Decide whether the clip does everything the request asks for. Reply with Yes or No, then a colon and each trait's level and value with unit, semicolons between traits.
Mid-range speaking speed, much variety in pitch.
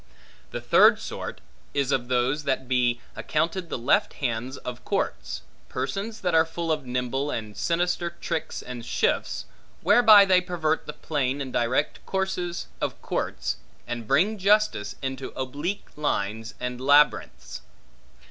Yes: average, 145 wpm; wide, 5.7 semitones